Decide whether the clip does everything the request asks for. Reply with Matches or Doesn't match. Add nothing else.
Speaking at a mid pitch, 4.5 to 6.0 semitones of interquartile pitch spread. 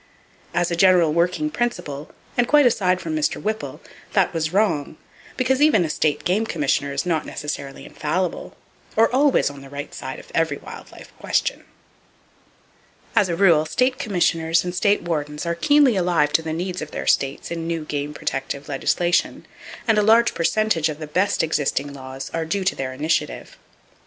Matches